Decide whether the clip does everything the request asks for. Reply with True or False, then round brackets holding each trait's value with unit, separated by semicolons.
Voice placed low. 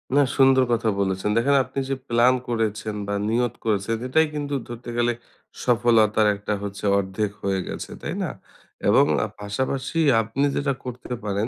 True (115 Hz)